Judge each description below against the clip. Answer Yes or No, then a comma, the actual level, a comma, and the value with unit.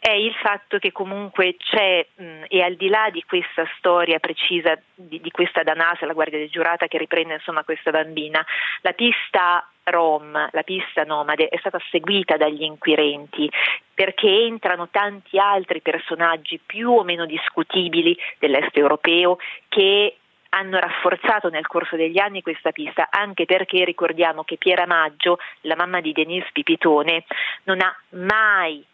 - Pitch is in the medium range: Yes, medium, 175 Hz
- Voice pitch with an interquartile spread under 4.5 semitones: Yes, average, 3.4 semitones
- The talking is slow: No, average, 150 wpm